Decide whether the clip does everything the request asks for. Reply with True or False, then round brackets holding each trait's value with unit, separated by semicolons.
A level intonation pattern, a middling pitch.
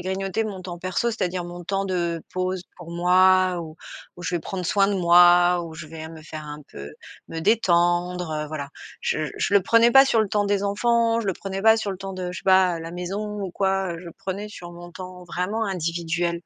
True (2.3 semitones; 180 Hz)